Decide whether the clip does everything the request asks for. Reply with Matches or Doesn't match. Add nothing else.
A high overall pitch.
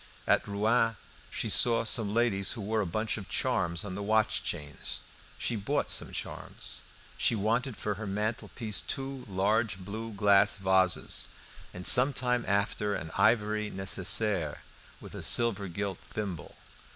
Doesn't match